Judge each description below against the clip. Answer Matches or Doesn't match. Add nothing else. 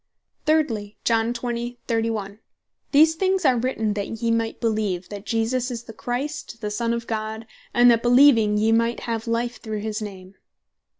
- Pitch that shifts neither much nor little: Doesn't match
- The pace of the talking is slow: Doesn't match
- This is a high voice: Matches